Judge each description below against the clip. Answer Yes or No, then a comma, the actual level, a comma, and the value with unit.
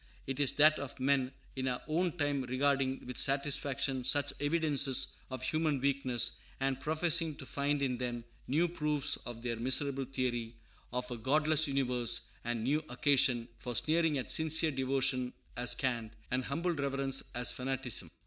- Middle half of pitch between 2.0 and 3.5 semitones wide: Yes, narrow, 2.5 semitones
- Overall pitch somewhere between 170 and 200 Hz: No, low, 135 Hz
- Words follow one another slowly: No, average, 160 wpm